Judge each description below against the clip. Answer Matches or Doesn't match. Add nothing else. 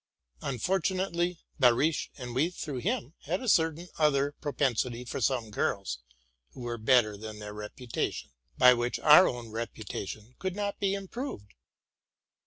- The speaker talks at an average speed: Matches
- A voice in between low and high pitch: Doesn't match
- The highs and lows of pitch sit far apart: Matches